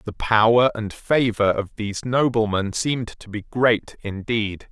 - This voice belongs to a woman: No, male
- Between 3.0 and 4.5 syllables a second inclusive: Yes, 4.2 syllables/s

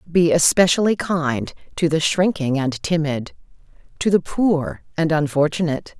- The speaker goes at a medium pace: No, slow, 130 wpm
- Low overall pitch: No, medium, 160 Hz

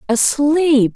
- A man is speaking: No, female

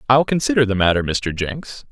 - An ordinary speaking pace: Yes, average, 190 wpm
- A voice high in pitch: No, low, 115 Hz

